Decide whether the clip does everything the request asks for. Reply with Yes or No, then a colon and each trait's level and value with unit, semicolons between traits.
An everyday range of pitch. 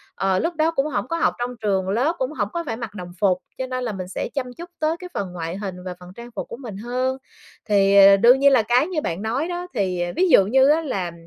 No: wide, 6.8 semitones